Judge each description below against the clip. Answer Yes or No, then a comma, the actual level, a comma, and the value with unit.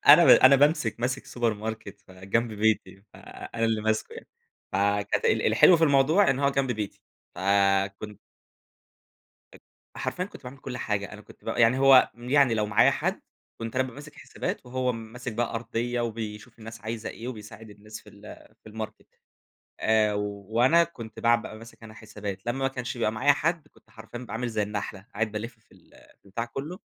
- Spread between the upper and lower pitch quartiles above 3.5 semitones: No, average, 3.1 semitones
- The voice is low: Yes, low, 115 Hz